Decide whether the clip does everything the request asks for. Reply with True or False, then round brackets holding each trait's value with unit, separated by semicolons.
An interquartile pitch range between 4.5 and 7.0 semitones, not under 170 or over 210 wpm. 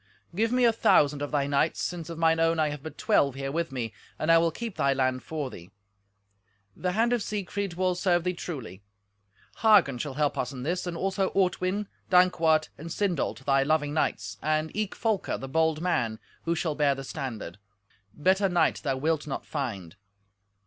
True (4.8 semitones; 190 wpm)